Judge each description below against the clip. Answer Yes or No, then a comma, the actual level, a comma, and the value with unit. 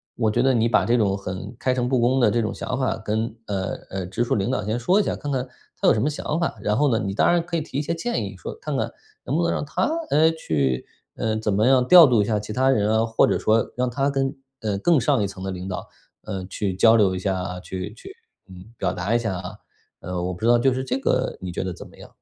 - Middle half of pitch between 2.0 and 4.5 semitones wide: No, average, 5.3 semitones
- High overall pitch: No, low, 110 Hz